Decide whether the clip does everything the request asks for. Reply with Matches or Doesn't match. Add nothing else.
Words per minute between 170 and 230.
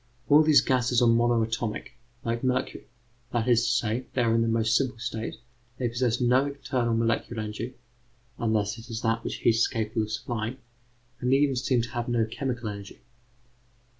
Matches